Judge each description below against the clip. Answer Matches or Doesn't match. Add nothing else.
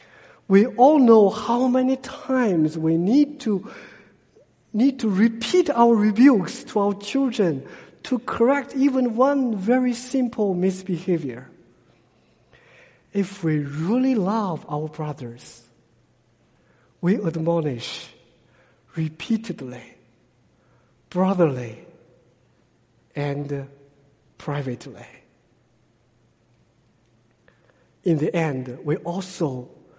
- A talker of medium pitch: Matches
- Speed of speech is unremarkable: Doesn't match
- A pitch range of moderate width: Doesn't match